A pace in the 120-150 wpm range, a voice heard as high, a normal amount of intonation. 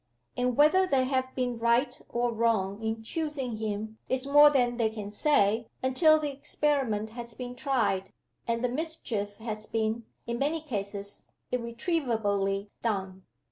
Yes: average, 145 wpm; high, 235 Hz; average, 3.7 semitones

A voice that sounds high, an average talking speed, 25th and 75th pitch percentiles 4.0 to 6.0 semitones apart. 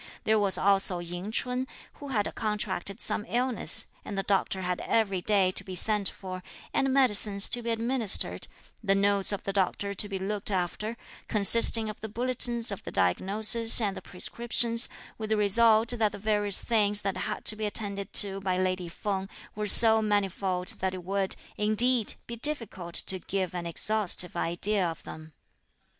No: high, 205 Hz; average, 175 wpm; average, 2.7 semitones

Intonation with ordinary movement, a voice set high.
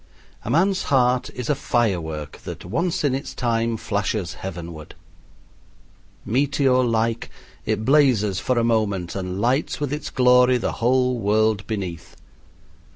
No: average, 4.5 semitones; low, 115 Hz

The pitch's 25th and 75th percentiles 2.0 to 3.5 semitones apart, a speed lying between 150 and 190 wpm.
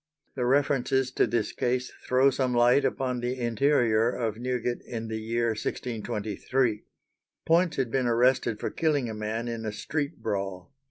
Yes: average, 2.7 semitones; average, 160 wpm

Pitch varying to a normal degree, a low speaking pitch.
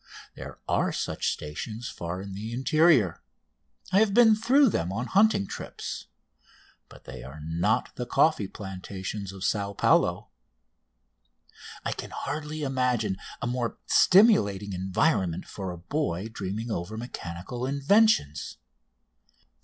No: wide, 7.9 semitones; low, 110 Hz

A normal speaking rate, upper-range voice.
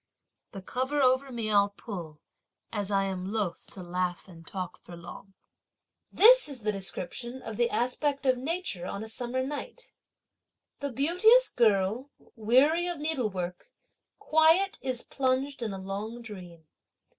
Yes: average, 145 wpm; high, 235 Hz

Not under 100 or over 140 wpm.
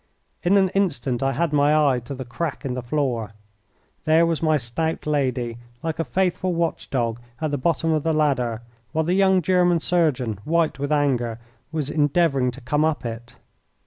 No: average, 185 wpm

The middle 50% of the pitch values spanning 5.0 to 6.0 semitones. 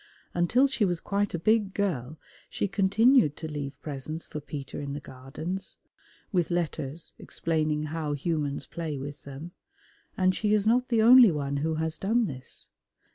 Yes: wide, 5.5 semitones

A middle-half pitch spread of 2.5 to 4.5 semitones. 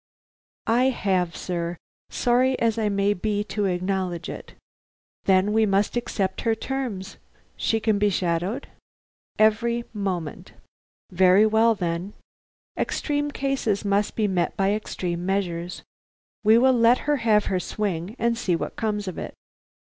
Yes: average, 3.5 semitones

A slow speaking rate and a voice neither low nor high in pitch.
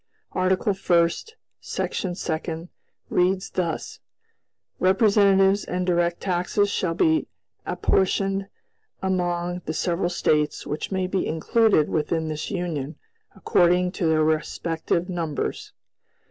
Yes: slow, 105 wpm; medium, 180 Hz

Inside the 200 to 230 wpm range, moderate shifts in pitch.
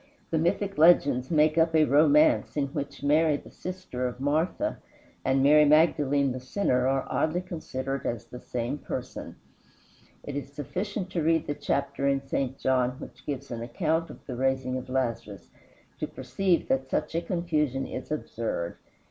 No: average, 165 wpm; average, 3.7 semitones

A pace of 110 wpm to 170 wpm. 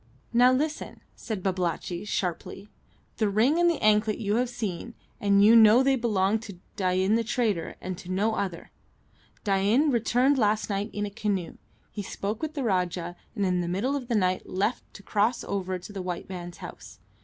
No: average, 190 wpm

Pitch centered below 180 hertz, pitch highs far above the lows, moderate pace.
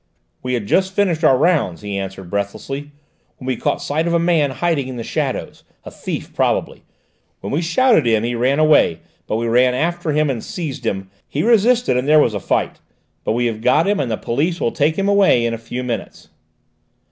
No: low, 135 Hz; wide, 6.2 semitones; fast, 215 wpm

